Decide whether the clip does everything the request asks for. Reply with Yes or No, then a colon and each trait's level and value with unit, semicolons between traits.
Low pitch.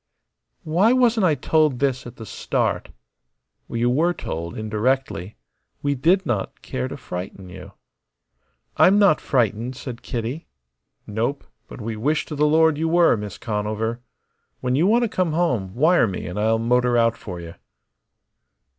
Yes: low, 125 Hz